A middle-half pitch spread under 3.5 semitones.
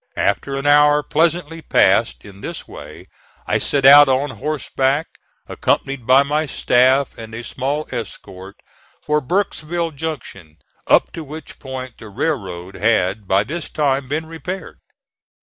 No: average, 5.2 semitones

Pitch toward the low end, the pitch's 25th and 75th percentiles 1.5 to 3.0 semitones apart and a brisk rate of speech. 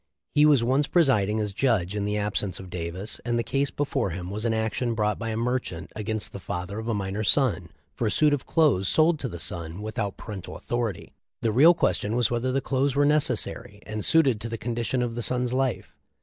No: low, 115 Hz; average, 4.1 semitones; fast, 220 wpm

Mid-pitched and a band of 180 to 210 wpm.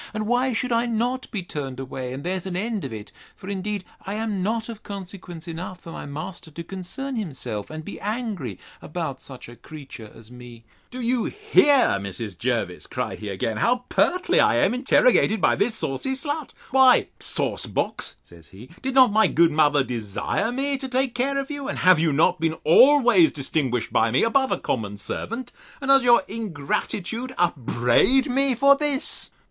No: high, 200 Hz; average, 185 wpm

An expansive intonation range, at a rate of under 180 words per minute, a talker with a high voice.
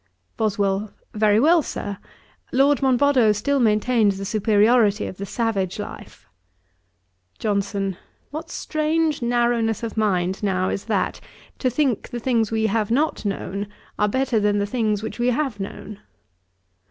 No: average, 3.6 semitones; average, 140 wpm; high, 220 Hz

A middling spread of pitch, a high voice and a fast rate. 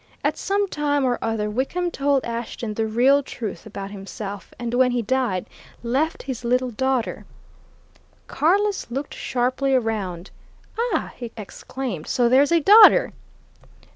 No: average, 4.1 semitones; very high, 250 Hz; average, 140 wpm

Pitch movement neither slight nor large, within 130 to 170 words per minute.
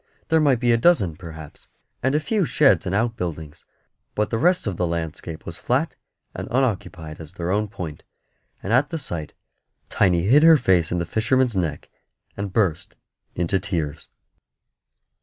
No: wide, 7.1 semitones; average, 165 wpm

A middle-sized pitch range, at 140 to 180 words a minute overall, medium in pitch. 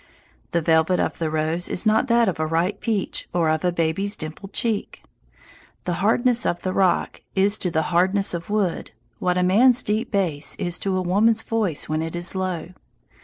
No: average, 3.7 semitones; average, 195 wpm; medium, 180 Hz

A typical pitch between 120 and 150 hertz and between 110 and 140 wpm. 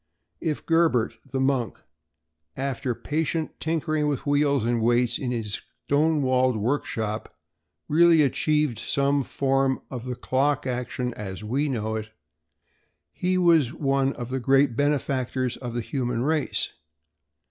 Yes: low, 135 Hz; slow, 135 wpm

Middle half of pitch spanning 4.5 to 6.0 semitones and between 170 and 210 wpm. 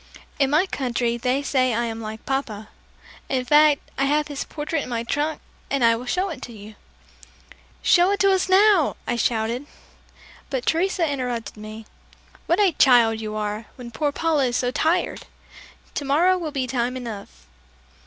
Yes: average, 4.8 semitones; average, 175 wpm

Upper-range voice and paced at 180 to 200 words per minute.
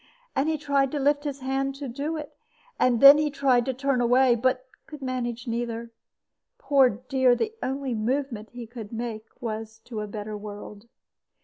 Yes: very high, 255 Hz; average, 185 wpm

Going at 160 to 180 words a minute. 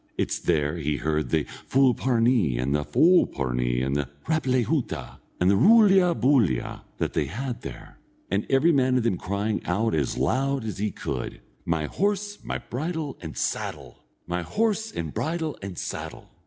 Yes: average, 165 wpm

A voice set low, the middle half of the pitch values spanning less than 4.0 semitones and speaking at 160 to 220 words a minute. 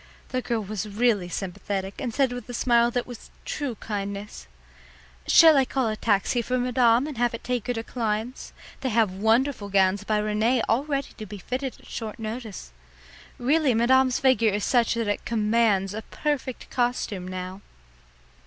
No: high, 230 Hz; average, 3.2 semitones; average, 175 wpm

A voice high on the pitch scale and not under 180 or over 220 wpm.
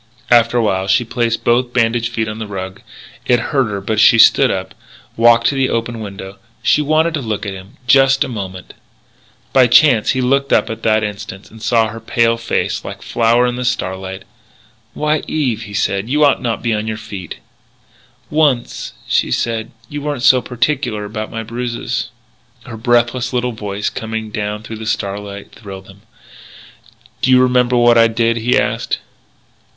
No: low, 115 Hz; average, 185 wpm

